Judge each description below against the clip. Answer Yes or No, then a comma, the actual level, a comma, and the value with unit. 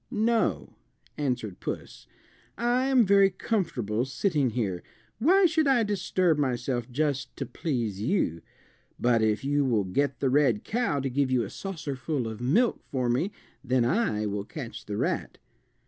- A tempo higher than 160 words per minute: No, average, 155 wpm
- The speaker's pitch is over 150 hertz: No, low, 135 Hz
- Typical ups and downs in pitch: No, wide, 8.3 semitones